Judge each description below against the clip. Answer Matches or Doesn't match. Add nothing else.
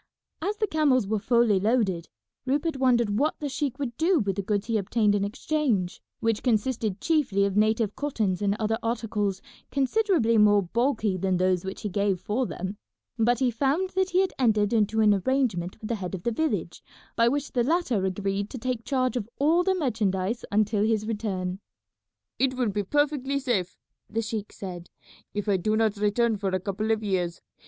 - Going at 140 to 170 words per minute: Doesn't match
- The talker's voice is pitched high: Matches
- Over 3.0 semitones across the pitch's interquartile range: Matches